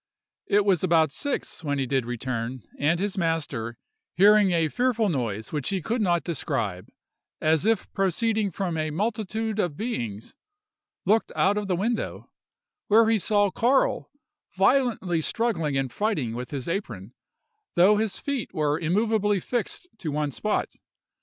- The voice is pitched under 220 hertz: Yes, medium, 185 Hz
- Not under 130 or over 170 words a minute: Yes, average, 145 wpm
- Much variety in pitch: Yes, wide, 6.8 semitones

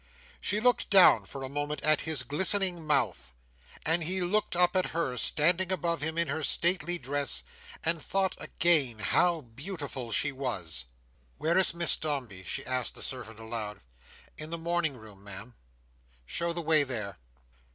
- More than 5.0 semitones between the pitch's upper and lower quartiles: Yes, wide, 5.5 semitones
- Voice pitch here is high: No, medium, 150 Hz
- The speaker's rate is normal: Yes, average, 160 wpm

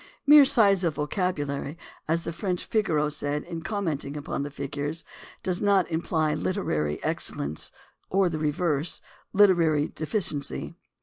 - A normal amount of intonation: Yes, average, 4.1 semitones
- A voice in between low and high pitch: Yes, medium, 160 Hz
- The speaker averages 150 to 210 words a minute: No, slow, 135 wpm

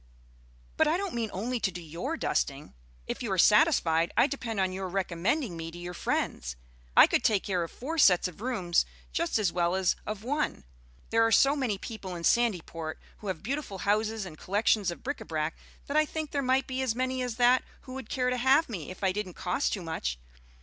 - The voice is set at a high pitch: Yes, high, 210 Hz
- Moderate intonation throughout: No, wide, 6.4 semitones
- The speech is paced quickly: Yes, fast, 220 wpm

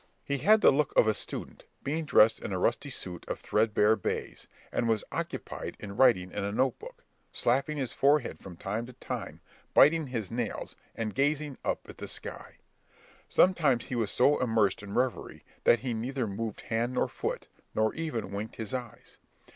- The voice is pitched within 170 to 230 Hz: No, low, 120 Hz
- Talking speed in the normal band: Yes, average, 185 wpm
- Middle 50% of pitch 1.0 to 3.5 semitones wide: No, average, 4.3 semitones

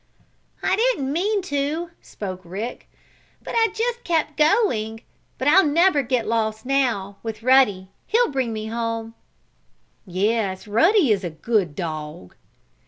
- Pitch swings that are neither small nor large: No, wide, 7.5 semitones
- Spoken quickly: No, slow, 135 wpm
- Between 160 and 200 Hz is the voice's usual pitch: No, high, 235 Hz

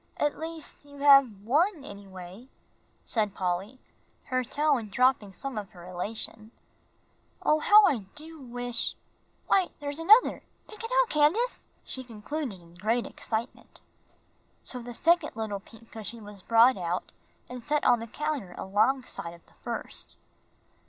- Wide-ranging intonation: Yes, wide, 6.1 semitones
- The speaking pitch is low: No, high, 245 Hz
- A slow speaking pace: No, average, 145 wpm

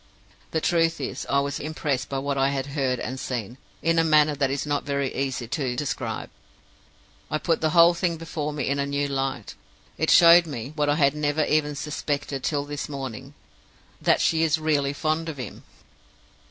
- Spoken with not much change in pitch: Yes, narrow, 2.3 semitones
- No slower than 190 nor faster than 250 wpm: Yes, average, 195 wpm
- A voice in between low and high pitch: Yes, medium, 145 Hz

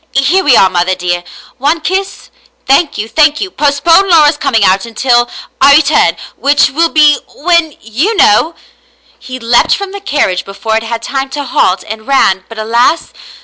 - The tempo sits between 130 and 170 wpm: No, average, 190 wpm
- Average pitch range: No, wide, 5.9 semitones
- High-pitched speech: Yes, very high, 275 Hz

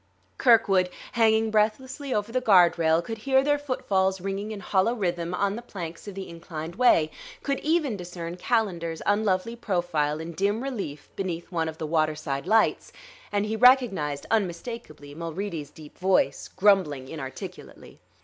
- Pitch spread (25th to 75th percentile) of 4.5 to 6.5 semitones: Yes, average, 5.1 semitones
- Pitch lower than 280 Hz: Yes, high, 190 Hz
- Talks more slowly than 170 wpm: Yes, average, 150 wpm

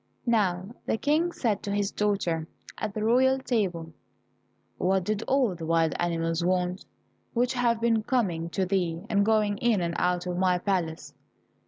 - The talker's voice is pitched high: Yes, high, 195 Hz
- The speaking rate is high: No, average, 165 wpm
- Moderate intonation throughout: Yes, average, 4.3 semitones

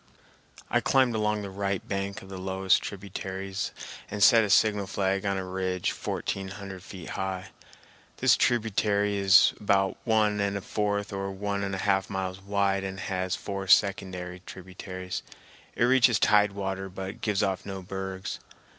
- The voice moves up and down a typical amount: No, narrow, 1.2 semitones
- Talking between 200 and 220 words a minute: No, average, 170 wpm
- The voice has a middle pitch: No, very low, 95 Hz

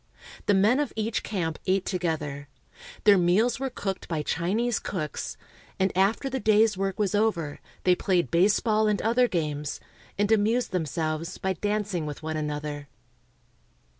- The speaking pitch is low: No, high, 190 Hz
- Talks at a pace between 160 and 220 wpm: No, average, 150 wpm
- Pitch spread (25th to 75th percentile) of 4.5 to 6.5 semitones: Yes, average, 4.8 semitones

